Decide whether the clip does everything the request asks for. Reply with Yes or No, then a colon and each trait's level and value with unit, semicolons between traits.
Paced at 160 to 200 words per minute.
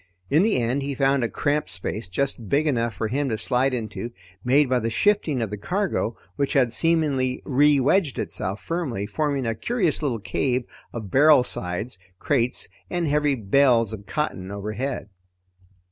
Yes: average, 165 wpm